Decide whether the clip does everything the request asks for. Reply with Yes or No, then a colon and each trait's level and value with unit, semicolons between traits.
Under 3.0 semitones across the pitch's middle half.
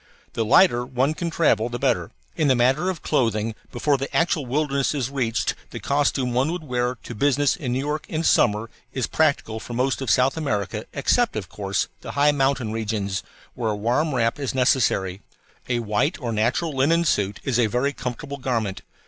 No: average, 4.0 semitones